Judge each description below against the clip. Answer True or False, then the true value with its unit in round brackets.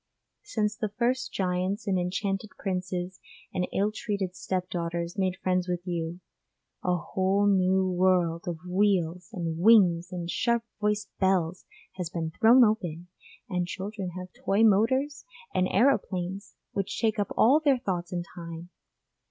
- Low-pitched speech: False (185 Hz)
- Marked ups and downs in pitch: False (2.8 semitones)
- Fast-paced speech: False (145 wpm)